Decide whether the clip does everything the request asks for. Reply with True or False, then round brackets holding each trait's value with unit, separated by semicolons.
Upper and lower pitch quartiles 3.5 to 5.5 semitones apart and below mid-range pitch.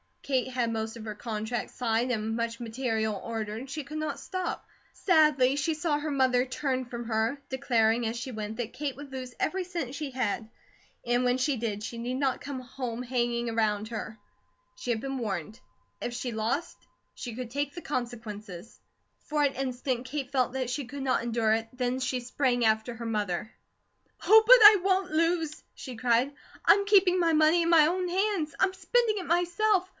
False (4.7 semitones; 255 Hz)